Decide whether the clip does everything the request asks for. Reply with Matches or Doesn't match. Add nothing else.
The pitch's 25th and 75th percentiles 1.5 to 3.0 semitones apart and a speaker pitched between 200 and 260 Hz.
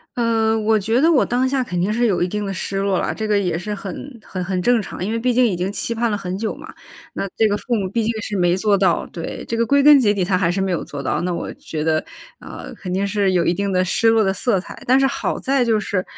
Doesn't match